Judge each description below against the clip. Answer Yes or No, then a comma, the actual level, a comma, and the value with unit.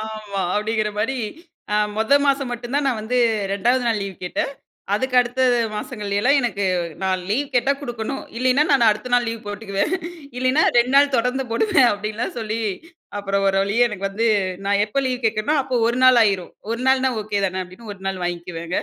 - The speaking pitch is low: No, high, 225 Hz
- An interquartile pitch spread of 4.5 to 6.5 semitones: No, average, 3.9 semitones